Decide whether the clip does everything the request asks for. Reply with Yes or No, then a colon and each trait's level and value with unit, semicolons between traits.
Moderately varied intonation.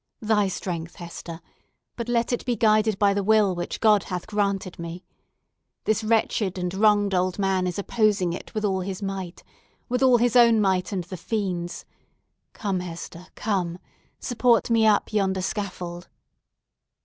Yes: average, 3.1 semitones